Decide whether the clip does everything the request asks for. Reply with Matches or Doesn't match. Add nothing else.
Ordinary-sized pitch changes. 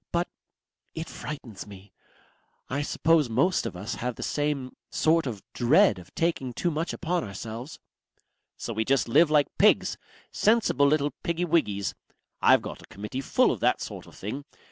Doesn't match